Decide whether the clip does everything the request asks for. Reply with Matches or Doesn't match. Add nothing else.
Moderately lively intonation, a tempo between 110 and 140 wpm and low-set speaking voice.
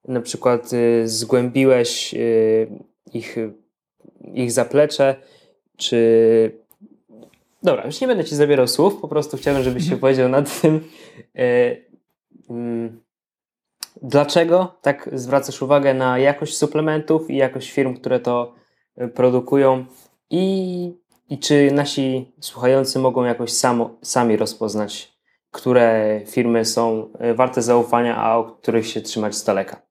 Matches